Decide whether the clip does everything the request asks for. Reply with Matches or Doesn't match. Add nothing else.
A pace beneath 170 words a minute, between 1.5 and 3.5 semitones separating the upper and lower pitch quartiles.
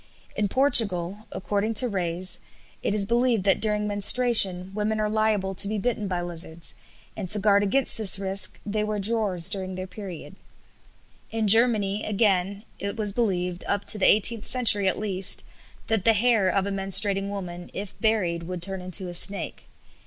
Doesn't match